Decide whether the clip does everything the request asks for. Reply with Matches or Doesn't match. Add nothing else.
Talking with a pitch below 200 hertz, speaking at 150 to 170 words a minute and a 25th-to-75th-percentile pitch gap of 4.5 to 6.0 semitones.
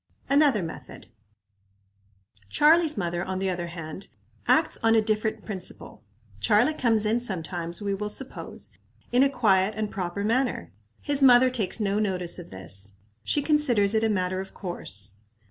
Doesn't match